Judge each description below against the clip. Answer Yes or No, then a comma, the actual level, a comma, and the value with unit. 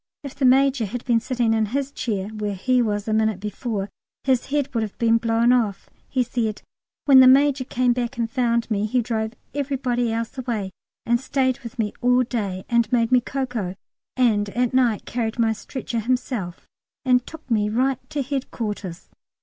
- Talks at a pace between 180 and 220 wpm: Yes, average, 185 wpm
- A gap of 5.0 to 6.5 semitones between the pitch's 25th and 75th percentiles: No, average, 2.7 semitones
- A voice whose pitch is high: Yes, high, 235 Hz